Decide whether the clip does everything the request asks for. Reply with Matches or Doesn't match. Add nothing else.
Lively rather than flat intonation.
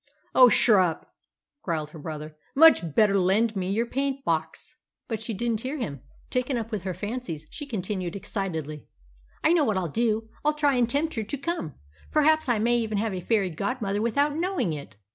Matches